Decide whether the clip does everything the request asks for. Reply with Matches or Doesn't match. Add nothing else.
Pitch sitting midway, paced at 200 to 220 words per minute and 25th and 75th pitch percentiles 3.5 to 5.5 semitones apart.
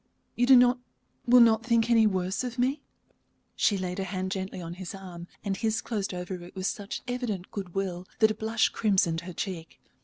Doesn't match